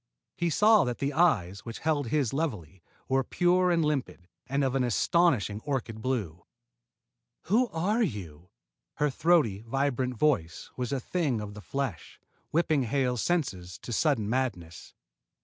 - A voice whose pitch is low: Yes, low, 130 Hz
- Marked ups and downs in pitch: Yes, wide, 6.7 semitones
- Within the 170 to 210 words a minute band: No, average, 150 wpm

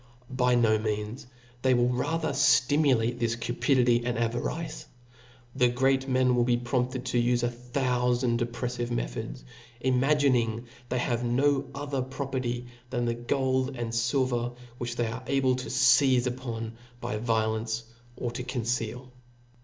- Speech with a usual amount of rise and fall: No, narrow, 1.6 semitones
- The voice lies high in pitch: No, low, 125 Hz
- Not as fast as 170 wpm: Yes, average, 145 wpm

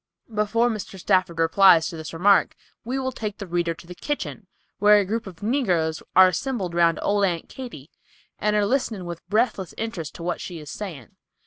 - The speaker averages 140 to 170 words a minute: No, average, 195 wpm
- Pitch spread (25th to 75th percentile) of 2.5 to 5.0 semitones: Yes, average, 4.1 semitones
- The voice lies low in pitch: No, high, 190 Hz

